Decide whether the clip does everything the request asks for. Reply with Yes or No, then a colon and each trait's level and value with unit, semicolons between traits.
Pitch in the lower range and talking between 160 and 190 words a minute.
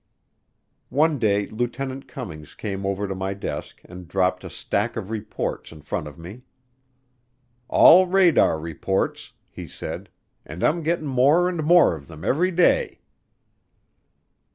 No: low, 110 Hz; average, 140 wpm